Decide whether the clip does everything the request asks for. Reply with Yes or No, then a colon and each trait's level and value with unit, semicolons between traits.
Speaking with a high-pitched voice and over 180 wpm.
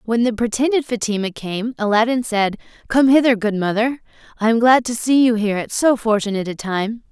Yes: high, 225 Hz; average, 195 wpm